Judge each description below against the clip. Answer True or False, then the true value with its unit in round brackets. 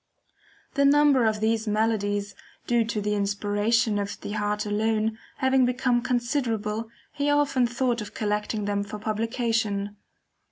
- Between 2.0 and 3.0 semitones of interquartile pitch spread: True (2.7 semitones)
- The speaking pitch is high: True (220 Hz)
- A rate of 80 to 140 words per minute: True (135 wpm)